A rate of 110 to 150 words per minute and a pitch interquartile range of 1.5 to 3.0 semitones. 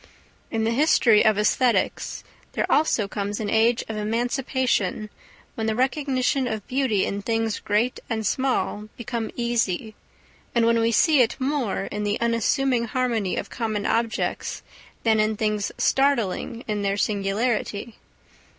Yes: average, 140 wpm; average, 2.7 semitones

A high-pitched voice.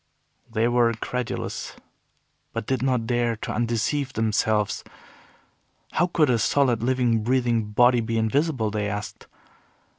No: low, 120 Hz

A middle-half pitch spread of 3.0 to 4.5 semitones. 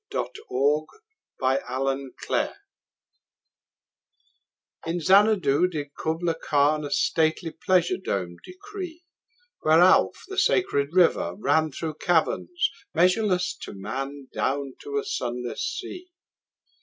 No: average, 5.2 semitones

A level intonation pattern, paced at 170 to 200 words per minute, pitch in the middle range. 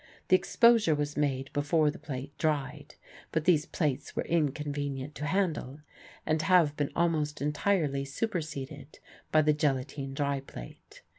No: narrow, 2.1 semitones; average, 140 wpm; medium, 150 Hz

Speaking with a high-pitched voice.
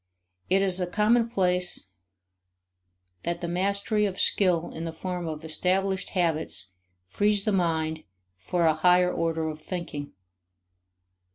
No: medium, 180 Hz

